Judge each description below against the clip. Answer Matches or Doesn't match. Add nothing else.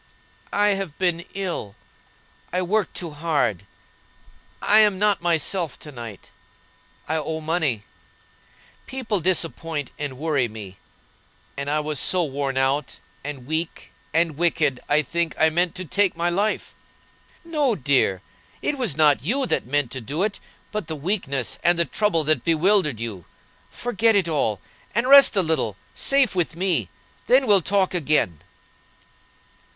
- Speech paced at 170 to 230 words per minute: Doesn't match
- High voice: Doesn't match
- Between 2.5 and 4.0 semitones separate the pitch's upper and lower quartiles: Doesn't match